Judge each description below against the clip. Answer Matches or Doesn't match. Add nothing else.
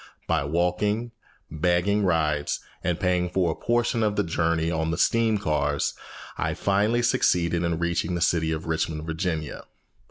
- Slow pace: Doesn't match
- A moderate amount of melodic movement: Matches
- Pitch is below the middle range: Matches